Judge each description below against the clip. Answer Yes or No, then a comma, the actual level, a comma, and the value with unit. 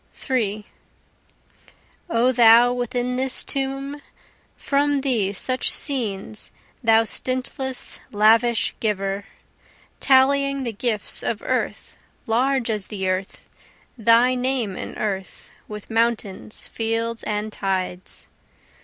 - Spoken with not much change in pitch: No, average, 3.6 semitones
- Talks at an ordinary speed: No, slow, 100 wpm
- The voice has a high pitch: Yes, high, 230 Hz